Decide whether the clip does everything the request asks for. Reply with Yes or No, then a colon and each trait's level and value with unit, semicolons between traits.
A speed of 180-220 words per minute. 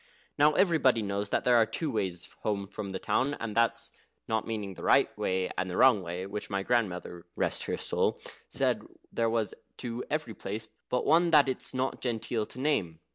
Yes: average, 190 wpm